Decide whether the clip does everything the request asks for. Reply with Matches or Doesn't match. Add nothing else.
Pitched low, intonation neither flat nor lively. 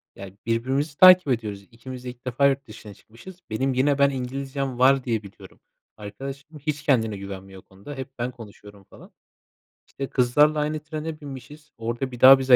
Matches